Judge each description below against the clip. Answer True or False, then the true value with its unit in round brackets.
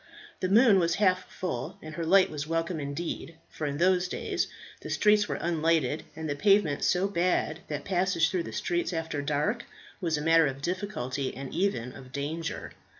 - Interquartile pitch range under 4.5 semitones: True (3.9 semitones)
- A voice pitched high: False (165 Hz)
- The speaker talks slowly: False (185 wpm)